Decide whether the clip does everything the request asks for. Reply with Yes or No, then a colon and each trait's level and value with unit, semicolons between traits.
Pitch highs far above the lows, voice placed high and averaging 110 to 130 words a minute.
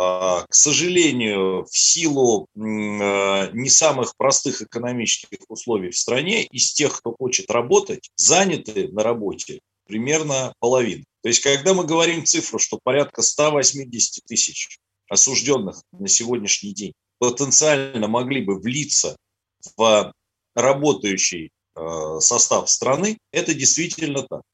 No: wide, 6.6 semitones; low, 130 Hz; average, 115 wpm